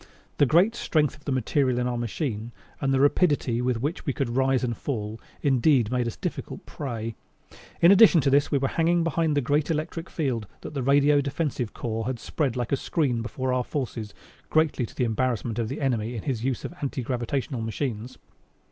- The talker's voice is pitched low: Yes, low, 130 Hz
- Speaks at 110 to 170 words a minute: No, fast, 205 wpm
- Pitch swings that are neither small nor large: Yes, average, 3.6 semitones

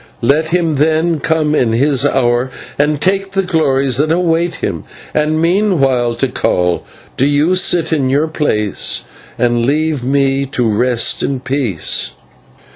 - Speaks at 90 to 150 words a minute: Yes, average, 140 wpm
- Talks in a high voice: No, medium, 145 Hz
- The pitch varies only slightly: No, average, 3.9 semitones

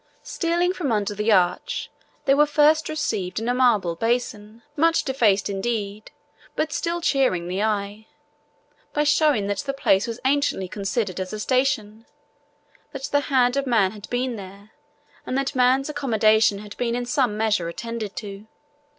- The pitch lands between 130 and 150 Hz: No, high, 230 Hz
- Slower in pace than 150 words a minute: No, average, 160 wpm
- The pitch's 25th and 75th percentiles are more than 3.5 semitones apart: Yes, average, 5.0 semitones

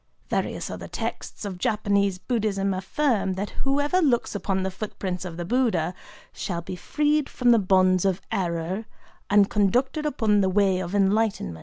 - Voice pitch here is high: Yes, high, 200 Hz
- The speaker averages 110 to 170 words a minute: Yes, average, 160 wpm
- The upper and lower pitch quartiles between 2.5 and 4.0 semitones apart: Yes, average, 3.7 semitones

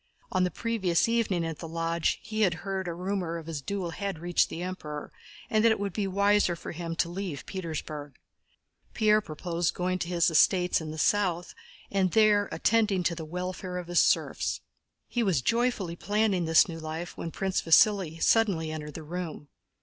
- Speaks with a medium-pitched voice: Yes, medium, 180 Hz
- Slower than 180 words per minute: No, average, 190 wpm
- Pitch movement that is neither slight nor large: Yes, average, 3.4 semitones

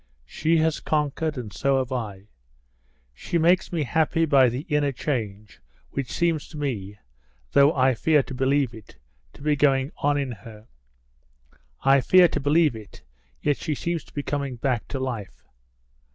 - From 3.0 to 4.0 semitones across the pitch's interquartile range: Yes, average, 3.6 semitones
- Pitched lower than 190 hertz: Yes, medium, 140 Hz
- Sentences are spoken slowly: No, average, 165 wpm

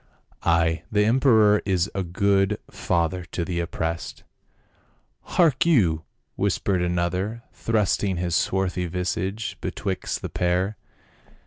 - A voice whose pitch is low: Yes, very low, 95 Hz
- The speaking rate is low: Yes, slow, 110 wpm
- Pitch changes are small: No, average, 3.1 semitones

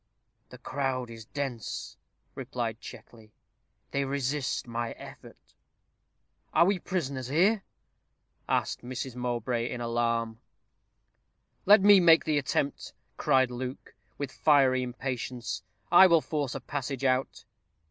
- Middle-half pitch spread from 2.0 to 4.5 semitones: Yes, average, 3.1 semitones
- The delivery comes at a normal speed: No, slow, 115 wpm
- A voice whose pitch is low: Yes, low, 130 Hz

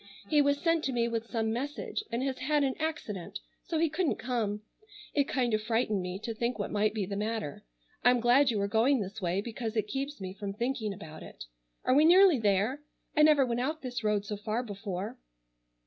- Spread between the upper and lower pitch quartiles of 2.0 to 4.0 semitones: No, average, 4.7 semitones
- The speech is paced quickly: Yes, fast, 215 wpm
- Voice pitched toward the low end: No, high, 235 Hz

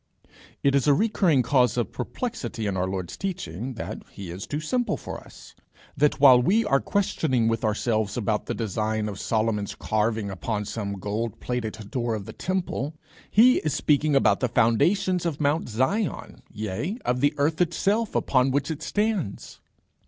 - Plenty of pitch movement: Yes, wide, 6.7 semitones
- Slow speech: No, average, 170 wpm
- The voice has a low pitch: Yes, low, 125 Hz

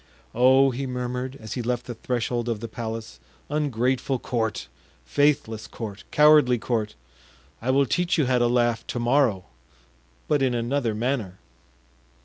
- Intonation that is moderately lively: Yes, average, 3.0 semitones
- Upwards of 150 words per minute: No, average, 140 wpm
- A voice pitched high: No, low, 120 Hz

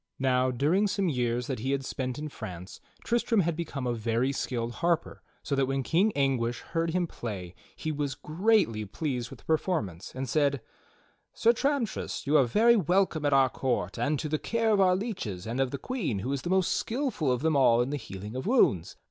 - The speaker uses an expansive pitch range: Yes, wide, 6.5 semitones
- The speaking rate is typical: No, fast, 210 wpm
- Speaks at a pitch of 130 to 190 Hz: Yes, medium, 140 Hz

